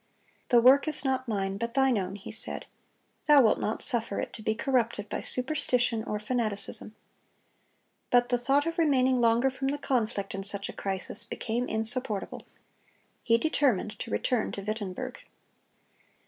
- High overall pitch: Yes, high, 235 Hz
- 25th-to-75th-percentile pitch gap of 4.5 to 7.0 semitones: No, average, 3.7 semitones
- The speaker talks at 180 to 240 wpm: No, average, 160 wpm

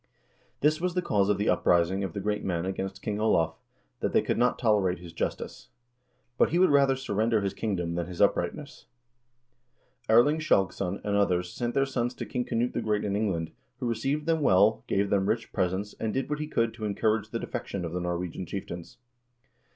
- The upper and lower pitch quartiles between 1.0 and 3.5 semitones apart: No, average, 4.6 semitones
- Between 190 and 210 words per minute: Yes, fast, 205 wpm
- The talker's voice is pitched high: No, low, 105 Hz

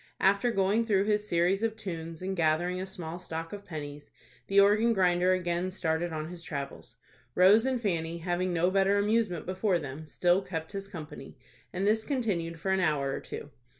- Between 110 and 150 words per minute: No, average, 185 wpm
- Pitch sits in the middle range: Yes, medium, 180 Hz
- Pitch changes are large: No, average, 3.4 semitones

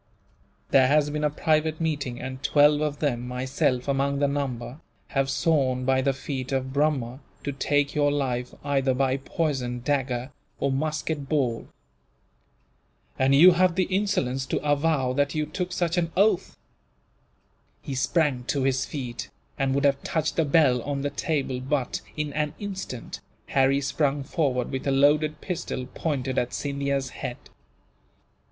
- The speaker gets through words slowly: No, average, 155 wpm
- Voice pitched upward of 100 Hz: Yes, medium, 140 Hz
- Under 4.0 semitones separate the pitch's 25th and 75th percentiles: Yes, narrow, 2.4 semitones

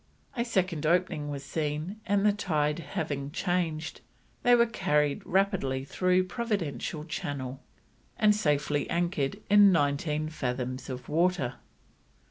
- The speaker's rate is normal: No, slow, 120 wpm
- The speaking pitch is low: No, medium, 155 Hz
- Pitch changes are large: No, average, 4.7 semitones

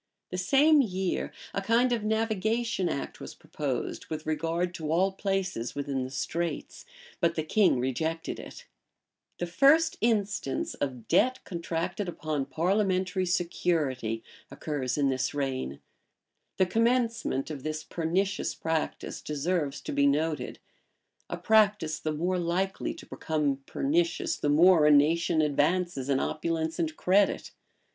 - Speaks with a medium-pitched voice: Yes, medium, 170 Hz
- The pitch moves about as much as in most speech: Yes, average, 4.7 semitones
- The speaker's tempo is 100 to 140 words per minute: Yes, slow, 135 wpm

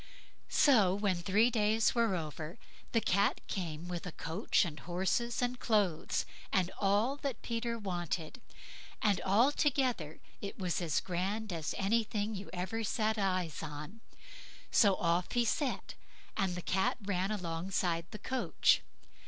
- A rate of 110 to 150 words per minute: Yes, average, 140 wpm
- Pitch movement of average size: Yes, average, 4.2 semitones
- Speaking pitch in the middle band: No, high, 195 Hz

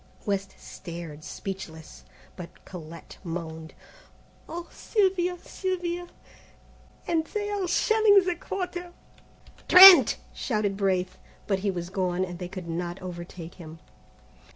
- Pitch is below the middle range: No, high, 195 Hz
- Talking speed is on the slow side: Yes, slow, 115 wpm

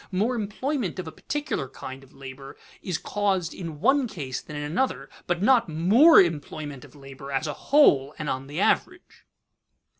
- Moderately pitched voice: Yes, medium, 165 Hz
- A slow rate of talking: No, average, 175 wpm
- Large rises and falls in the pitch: Yes, wide, 7.1 semitones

